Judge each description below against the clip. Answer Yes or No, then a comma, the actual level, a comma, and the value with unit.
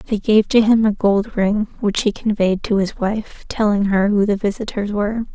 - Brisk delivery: Yes, fast, 215 wpm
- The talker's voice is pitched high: Yes, high, 210 Hz